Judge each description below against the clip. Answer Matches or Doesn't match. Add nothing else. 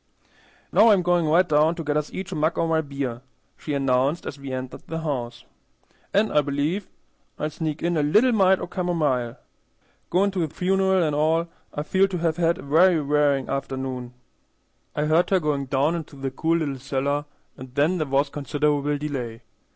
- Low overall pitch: Doesn't match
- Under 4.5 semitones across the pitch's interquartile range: Matches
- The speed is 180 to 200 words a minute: Matches